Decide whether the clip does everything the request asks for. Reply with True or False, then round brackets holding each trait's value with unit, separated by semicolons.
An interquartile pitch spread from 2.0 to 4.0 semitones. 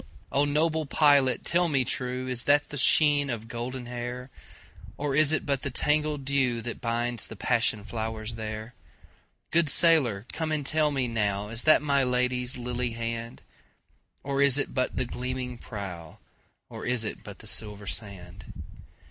True (3.7 semitones)